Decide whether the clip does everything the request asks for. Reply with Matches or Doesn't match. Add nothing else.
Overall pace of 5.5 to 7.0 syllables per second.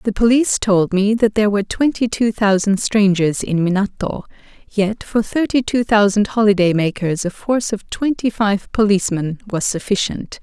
Doesn't match